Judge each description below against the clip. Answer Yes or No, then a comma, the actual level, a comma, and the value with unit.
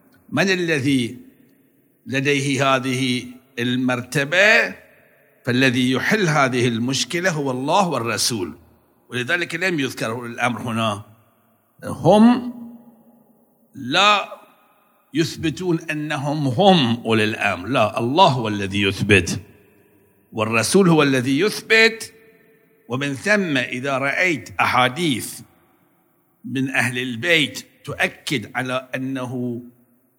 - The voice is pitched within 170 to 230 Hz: No, low, 135 Hz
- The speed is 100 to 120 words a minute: No, average, 85 wpm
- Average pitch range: No, wide, 6.4 semitones